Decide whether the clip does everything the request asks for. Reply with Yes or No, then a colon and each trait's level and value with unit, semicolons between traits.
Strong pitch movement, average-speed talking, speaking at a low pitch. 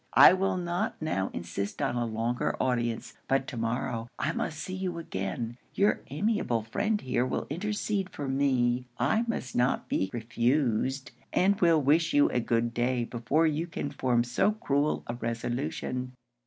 Yes: wide, 5.9 semitones; average, 165 wpm; low, 130 Hz